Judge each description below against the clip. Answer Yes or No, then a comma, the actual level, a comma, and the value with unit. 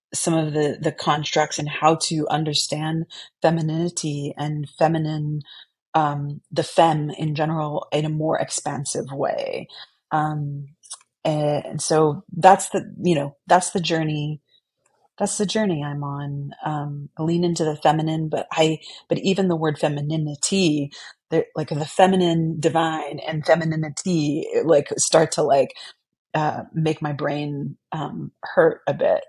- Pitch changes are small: Yes, narrow, 2.0 semitones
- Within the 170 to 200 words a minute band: No, average, 140 wpm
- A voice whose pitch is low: No, medium, 155 Hz